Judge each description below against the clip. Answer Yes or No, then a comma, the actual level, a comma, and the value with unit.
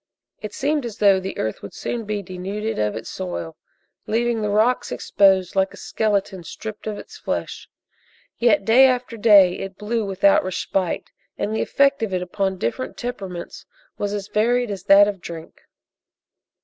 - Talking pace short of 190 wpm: Yes, average, 170 wpm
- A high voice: Yes, high, 205 Hz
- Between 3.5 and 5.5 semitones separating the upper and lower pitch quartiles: No, average, 3.0 semitones